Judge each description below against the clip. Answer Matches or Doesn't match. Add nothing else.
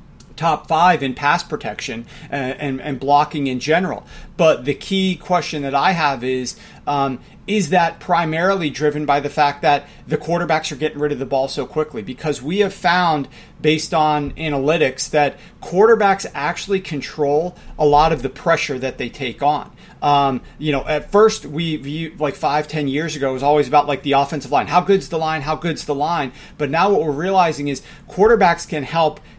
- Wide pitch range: Doesn't match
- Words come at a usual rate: Matches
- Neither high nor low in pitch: Matches